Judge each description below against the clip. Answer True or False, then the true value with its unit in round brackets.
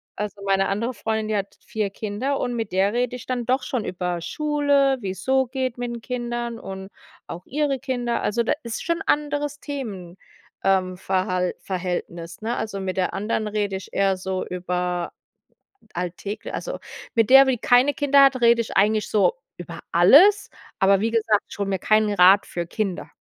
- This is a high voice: True (215 Hz)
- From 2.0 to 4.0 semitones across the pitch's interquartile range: False (4.8 semitones)